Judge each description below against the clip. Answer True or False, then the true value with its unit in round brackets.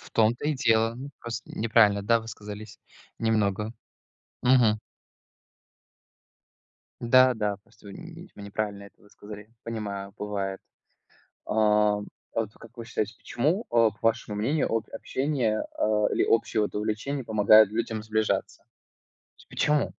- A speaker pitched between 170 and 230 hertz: False (110 Hz)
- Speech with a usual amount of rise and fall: False (2.2 semitones)